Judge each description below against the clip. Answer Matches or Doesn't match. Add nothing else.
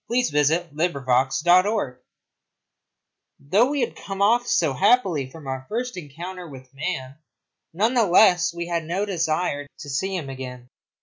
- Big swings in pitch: Matches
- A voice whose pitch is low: Doesn't match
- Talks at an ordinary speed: Matches